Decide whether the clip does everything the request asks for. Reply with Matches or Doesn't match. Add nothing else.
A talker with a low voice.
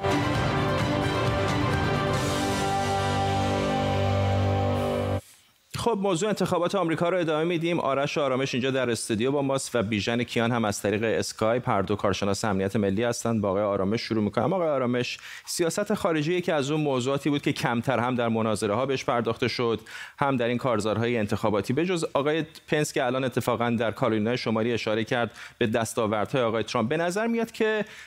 Matches